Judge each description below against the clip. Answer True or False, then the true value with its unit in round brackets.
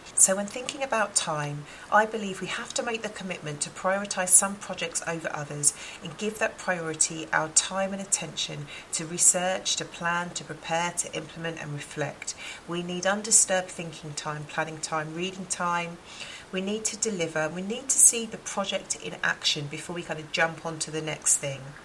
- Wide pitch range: False (3.7 semitones)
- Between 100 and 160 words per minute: False (185 wpm)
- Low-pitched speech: False (175 Hz)